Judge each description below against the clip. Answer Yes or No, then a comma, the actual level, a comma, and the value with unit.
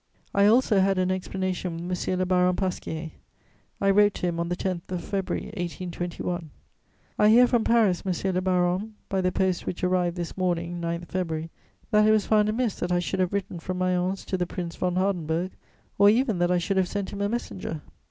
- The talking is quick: Yes, fast, 210 wpm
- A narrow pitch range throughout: Yes, narrow, 2.2 semitones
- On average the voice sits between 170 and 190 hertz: Yes, medium, 185 Hz